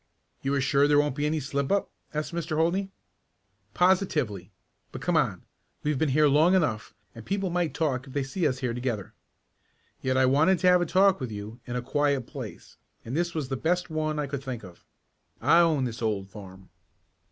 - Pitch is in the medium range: Yes, medium, 145 Hz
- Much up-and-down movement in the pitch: No, average, 4.4 semitones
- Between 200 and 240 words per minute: Yes, fast, 205 wpm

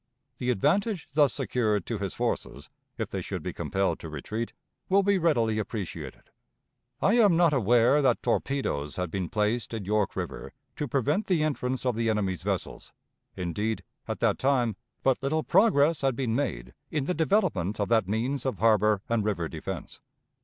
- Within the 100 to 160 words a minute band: No, average, 175 wpm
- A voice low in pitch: Yes, low, 115 Hz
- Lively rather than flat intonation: Yes, wide, 5.8 semitones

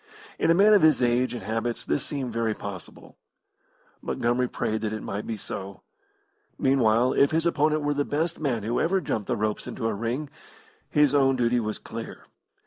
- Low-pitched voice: Yes, low, 125 Hz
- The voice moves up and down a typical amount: Yes, average, 4.7 semitones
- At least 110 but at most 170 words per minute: No, average, 190 wpm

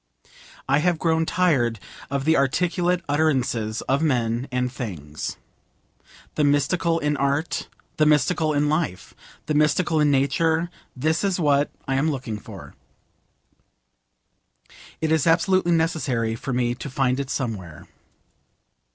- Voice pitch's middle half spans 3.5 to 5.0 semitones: Yes, average, 4.2 semitones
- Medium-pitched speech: Yes, medium, 145 Hz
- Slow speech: Yes, slow, 130 wpm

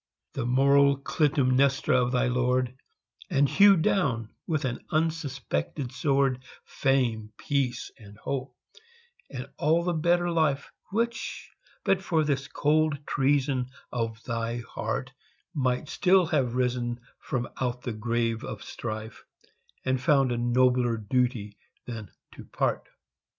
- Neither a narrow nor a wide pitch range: Yes, average, 3.2 semitones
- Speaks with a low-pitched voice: Yes, low, 130 Hz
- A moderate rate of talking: No, slow, 125 wpm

